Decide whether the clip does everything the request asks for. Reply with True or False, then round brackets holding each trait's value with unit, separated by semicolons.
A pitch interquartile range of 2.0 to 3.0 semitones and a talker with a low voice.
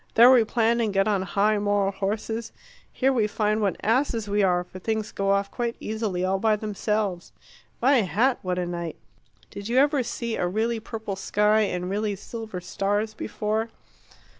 False (2.4 semitones; 210 Hz)